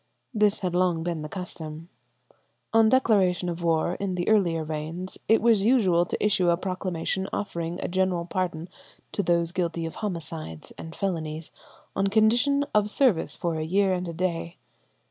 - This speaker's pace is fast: No, average, 165 wpm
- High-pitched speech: No, medium, 180 Hz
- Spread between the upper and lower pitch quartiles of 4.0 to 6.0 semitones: No, average, 3.2 semitones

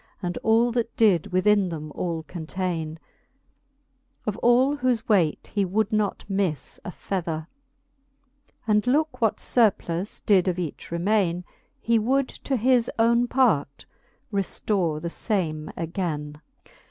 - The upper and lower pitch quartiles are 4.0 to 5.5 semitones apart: Yes, average, 5.2 semitones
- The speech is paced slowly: Yes, slow, 130 wpm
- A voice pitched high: Yes, high, 195 Hz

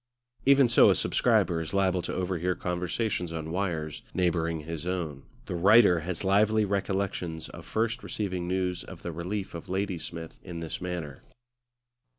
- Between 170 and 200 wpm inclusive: No, average, 155 wpm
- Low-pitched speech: Yes, very low, 90 Hz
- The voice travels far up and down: No, average, 2.8 semitones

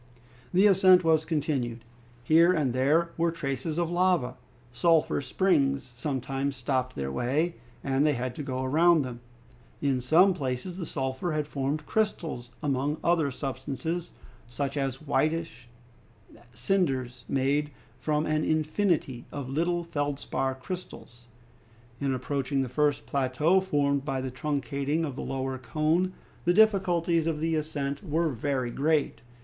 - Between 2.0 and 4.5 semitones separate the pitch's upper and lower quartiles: Yes, average, 3.9 semitones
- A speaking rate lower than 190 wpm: Yes, average, 140 wpm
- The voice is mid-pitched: Yes, medium, 145 Hz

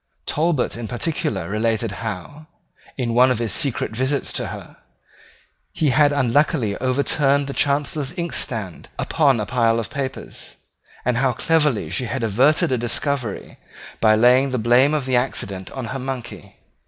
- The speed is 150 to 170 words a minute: Yes, average, 155 wpm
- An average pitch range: Yes, average, 3.7 semitones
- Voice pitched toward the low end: Yes, low, 125 Hz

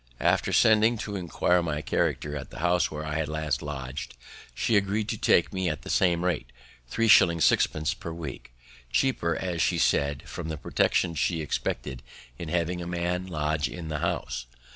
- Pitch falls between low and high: No, very low, 85 Hz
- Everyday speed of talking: Yes, average, 180 wpm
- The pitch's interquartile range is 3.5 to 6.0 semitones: No, average, 3.0 semitones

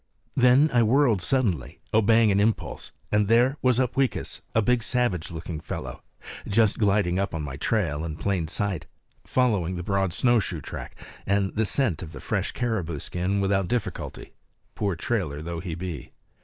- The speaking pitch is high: No, low, 100 Hz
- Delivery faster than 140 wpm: Yes, average, 165 wpm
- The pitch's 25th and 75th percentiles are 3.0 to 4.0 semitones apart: No, average, 5.2 semitones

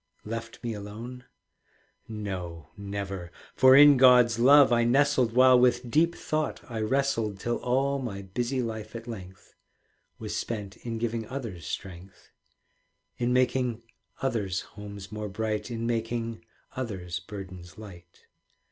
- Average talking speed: No, slow, 130 wpm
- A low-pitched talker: Yes, low, 115 Hz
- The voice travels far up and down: No, average, 3.7 semitones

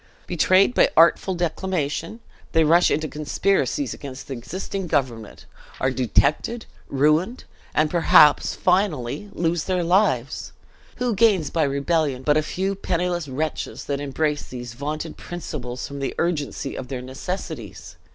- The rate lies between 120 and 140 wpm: Yes, slow, 135 wpm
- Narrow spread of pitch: No, average, 4.6 semitones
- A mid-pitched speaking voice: Yes, medium, 155 Hz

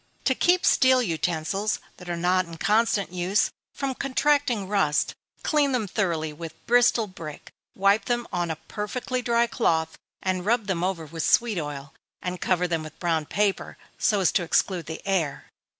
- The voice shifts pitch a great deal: Yes, wide, 5.8 semitones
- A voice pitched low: No, high, 190 Hz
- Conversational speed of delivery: Yes, average, 170 wpm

